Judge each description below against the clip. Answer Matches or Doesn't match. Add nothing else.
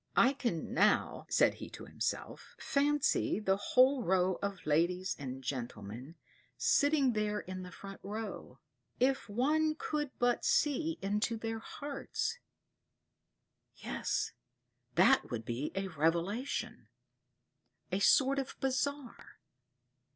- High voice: Matches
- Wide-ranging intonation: Matches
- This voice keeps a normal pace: Doesn't match